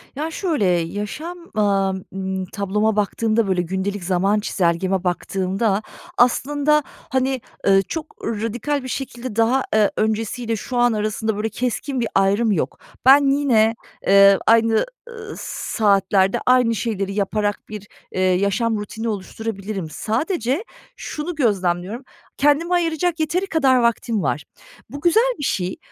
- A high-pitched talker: Yes, high, 220 Hz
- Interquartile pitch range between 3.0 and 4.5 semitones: No, average, 5.0 semitones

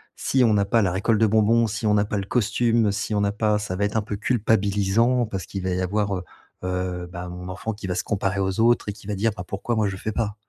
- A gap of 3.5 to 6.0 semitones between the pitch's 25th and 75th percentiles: No, narrow, 2.5 semitones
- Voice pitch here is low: Yes, low, 105 Hz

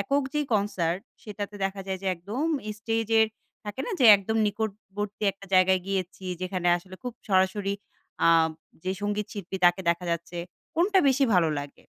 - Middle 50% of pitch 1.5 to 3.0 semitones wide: Yes, average, 2.7 semitones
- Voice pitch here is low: No, high, 200 Hz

